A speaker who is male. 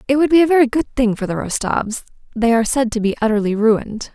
No: female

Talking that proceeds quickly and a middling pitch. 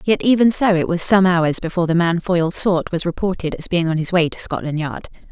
Yes: fast, 250 wpm; medium, 175 Hz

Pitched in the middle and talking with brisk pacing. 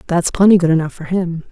Yes: medium, 175 Hz; fast, 240 wpm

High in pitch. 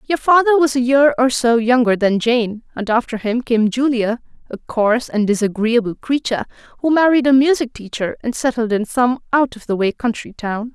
Yes: high, 240 Hz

